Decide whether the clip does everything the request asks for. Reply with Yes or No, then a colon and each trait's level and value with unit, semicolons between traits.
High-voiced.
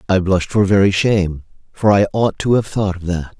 No: very low, 95 Hz